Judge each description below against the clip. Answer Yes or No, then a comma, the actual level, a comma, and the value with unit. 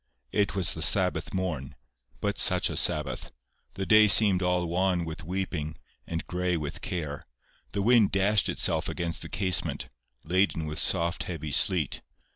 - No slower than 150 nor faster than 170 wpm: Yes, average, 155 wpm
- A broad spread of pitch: No, average, 3.4 semitones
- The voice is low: Yes, very low, 90 Hz